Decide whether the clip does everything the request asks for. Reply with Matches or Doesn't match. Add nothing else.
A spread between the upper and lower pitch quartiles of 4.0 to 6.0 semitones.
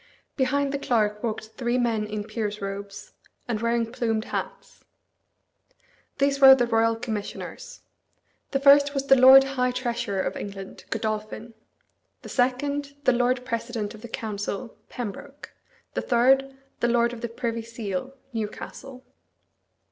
Doesn't match